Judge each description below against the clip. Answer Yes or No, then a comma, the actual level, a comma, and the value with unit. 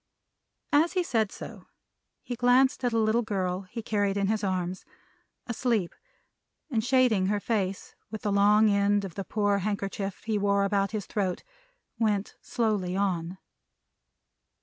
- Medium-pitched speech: No, high, 205 Hz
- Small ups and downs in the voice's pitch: Yes, narrow, 2.3 semitones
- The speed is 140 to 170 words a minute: Yes, average, 150 wpm